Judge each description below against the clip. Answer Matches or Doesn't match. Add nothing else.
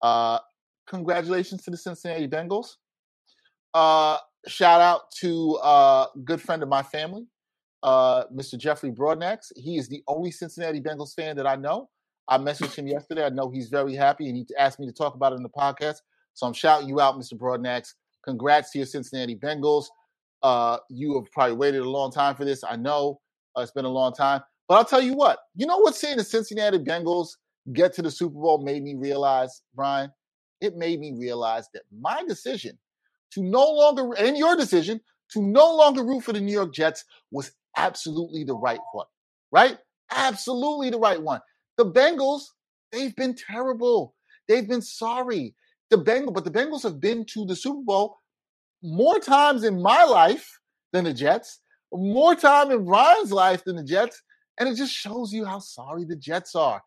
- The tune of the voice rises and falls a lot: Matches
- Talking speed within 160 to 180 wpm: Doesn't match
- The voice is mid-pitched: Matches